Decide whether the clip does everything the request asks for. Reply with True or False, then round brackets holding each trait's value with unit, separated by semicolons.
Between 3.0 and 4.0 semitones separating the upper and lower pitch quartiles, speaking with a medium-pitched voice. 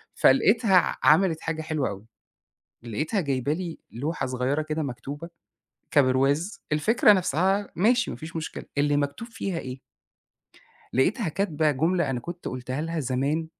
False (4.7 semitones; 155 Hz)